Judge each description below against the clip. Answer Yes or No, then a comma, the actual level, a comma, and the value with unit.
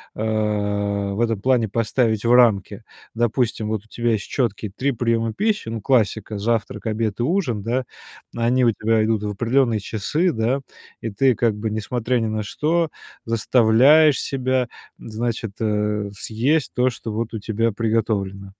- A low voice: Yes, low, 115 Hz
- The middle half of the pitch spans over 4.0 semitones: No, narrow, 2.5 semitones